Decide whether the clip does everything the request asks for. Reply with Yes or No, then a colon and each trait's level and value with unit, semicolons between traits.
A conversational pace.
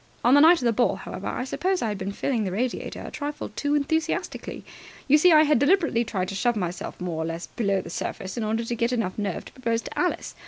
No: fast, 250 wpm